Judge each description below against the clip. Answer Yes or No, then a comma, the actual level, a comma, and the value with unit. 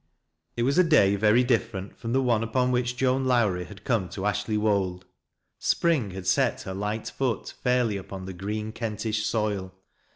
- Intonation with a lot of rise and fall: No, average, 3.8 semitones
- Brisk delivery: No, average, 175 wpm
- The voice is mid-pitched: No, low, 110 Hz